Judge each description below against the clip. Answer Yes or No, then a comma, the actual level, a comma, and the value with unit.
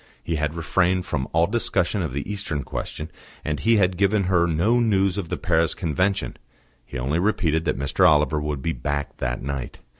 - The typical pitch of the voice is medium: No, very low, 80 Hz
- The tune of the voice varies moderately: Yes, average, 4.4 semitones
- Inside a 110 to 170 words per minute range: No, average, 190 wpm